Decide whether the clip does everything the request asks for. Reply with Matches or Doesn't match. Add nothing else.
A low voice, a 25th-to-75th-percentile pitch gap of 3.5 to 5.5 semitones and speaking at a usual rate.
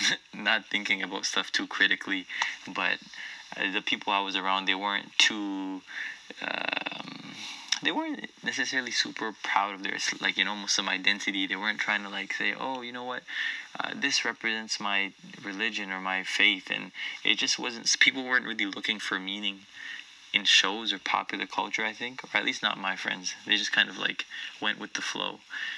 Doesn't match